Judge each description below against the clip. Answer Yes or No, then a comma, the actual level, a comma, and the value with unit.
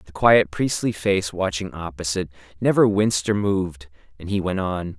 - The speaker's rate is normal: Yes, average, 170 wpm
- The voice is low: Yes, very low, 95 Hz